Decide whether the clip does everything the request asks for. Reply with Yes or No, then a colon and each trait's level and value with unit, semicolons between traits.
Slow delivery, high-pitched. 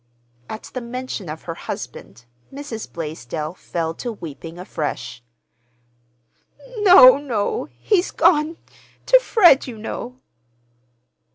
Yes: slow, 100 wpm; high, 225 Hz